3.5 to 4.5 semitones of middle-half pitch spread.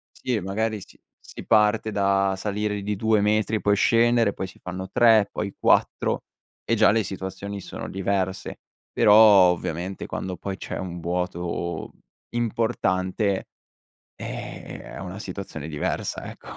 No: narrow, 2.4 semitones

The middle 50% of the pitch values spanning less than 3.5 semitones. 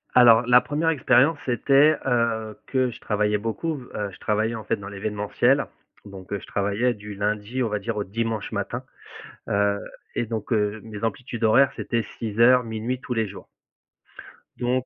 Yes: average, 3.0 semitones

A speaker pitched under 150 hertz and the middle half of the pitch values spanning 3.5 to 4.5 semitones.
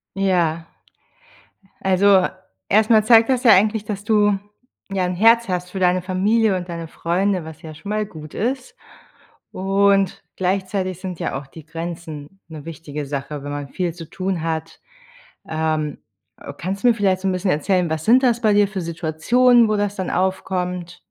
No: medium, 185 Hz; average, 3.8 semitones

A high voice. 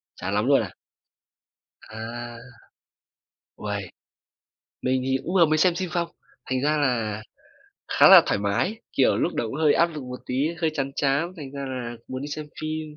No: medium, 140 Hz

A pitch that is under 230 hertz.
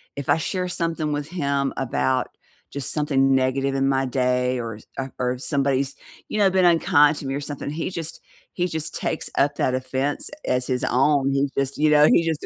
Yes: medium, 140 Hz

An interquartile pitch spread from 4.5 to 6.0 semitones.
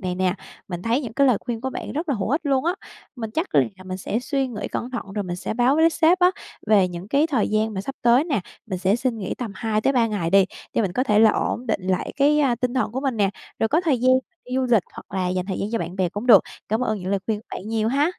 Yes: average, 5.0 semitones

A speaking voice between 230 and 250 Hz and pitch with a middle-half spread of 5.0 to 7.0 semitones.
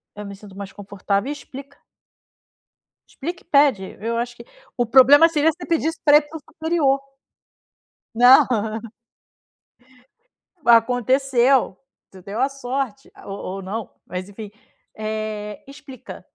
Yes: high, 245 Hz; average, 5.3 semitones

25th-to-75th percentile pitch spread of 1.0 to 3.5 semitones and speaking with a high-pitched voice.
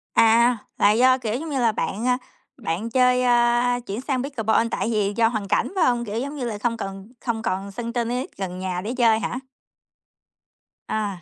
Yes: average, 3.1 semitones; high, 230 Hz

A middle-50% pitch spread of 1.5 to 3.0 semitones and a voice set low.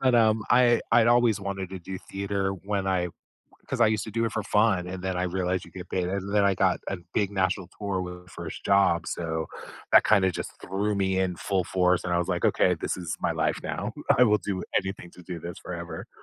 Yes: narrow, 2.4 semitones; very low, 95 Hz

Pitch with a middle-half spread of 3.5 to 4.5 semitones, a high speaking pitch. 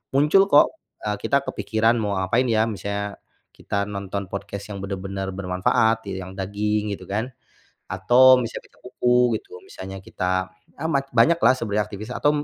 No: average, 4.0 semitones; low, 105 Hz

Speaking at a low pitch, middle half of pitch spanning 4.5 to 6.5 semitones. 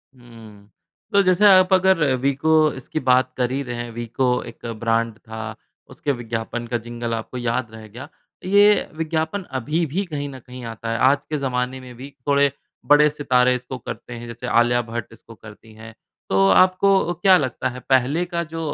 Yes: low, 125 Hz; average, 4.8 semitones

